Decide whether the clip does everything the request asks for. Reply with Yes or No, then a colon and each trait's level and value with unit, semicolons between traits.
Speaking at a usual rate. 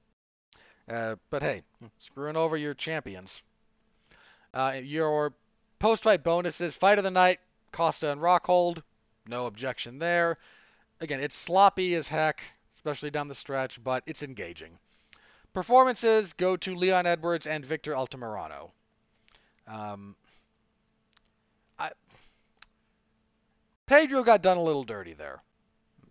No: slow, 115 wpm